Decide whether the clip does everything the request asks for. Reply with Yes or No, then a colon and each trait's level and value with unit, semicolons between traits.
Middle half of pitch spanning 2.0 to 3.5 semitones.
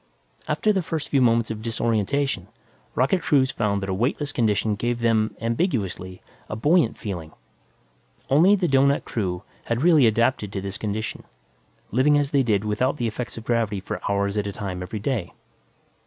No: average, 5.1 semitones